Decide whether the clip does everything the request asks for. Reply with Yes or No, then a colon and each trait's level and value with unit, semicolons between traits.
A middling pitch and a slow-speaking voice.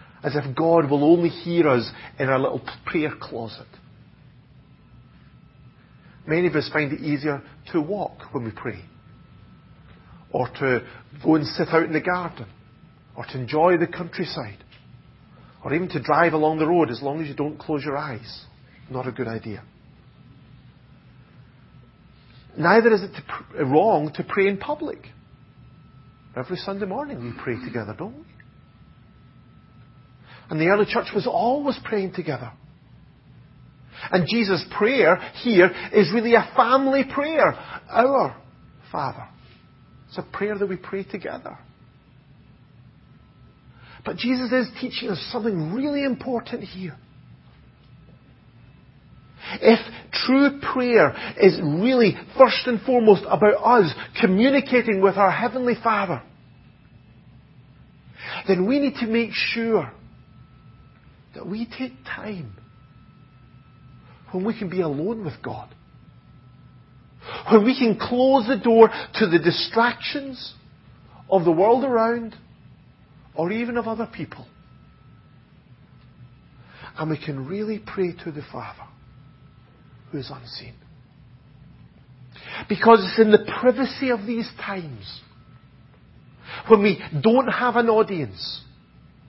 Yes: medium, 175 Hz; slow, 125 wpm